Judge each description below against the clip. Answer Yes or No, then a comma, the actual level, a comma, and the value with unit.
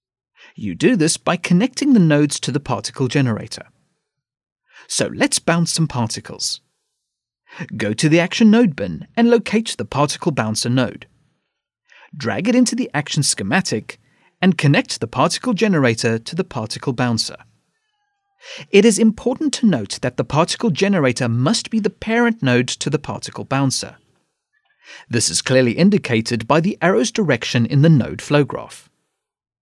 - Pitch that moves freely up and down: Yes, wide, 8.9 semitones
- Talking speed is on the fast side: No, average, 150 wpm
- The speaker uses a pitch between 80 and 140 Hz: No, medium, 150 Hz